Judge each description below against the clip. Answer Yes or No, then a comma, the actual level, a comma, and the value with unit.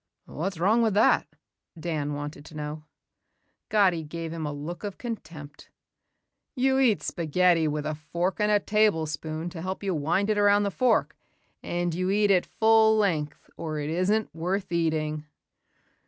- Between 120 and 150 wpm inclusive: No, average, 160 wpm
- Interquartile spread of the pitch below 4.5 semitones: No, average, 4.8 semitones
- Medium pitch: Yes, medium, 175 Hz